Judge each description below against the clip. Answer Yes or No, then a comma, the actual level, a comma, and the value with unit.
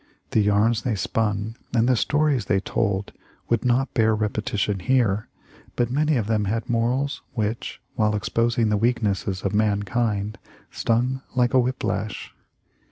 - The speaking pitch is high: No, low, 110 Hz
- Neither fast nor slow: Yes, average, 150 wpm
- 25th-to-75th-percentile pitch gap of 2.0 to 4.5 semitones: Yes, average, 2.8 semitones